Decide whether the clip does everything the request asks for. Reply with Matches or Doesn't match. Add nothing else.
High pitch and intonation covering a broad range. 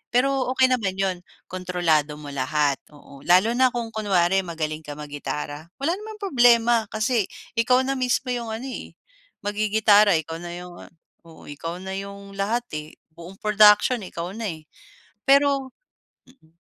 Matches